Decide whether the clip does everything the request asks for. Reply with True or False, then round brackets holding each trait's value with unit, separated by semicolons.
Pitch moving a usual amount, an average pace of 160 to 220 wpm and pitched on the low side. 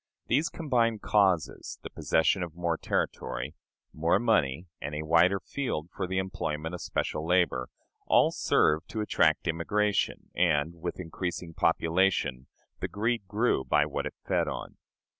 False (4.2 semitones; 145 wpm; 90 Hz)